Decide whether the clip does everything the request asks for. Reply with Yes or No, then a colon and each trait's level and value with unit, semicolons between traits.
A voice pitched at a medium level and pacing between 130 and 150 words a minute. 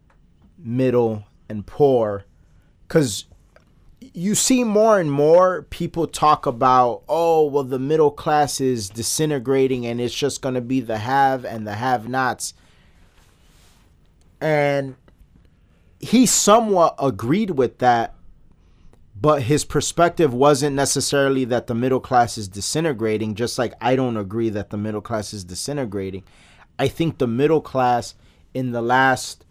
No: low, 130 Hz; slow, 135 wpm